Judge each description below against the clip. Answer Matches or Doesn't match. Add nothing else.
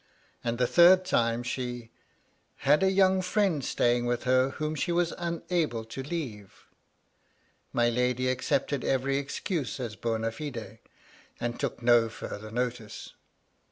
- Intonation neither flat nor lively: Matches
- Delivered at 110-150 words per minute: Matches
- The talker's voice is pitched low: Matches